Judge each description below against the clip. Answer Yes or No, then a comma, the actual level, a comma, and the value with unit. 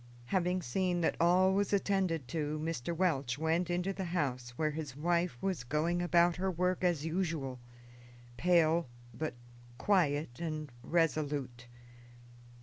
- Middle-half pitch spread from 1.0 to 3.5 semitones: Yes, average, 3.2 semitones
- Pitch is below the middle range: No, medium, 165 Hz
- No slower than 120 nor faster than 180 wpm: Yes, slow, 135 wpm